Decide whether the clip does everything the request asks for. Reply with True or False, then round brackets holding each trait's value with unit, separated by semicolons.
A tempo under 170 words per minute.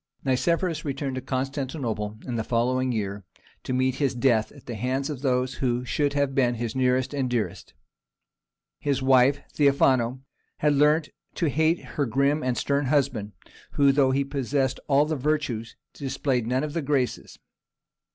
True (160 wpm)